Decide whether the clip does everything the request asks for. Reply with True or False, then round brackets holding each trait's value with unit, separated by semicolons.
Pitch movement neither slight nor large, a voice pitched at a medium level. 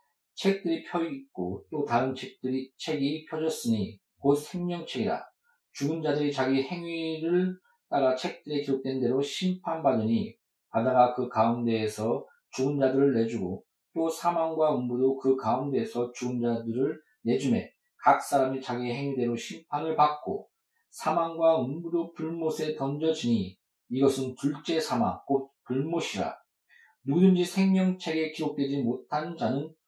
True (4.4 semitones; 145 Hz)